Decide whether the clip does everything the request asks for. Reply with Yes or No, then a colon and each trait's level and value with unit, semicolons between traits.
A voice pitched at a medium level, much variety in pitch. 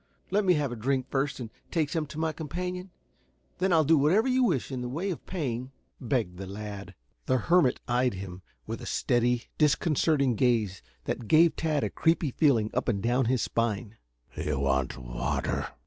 No: low, 130 Hz; wide, 6.1 semitones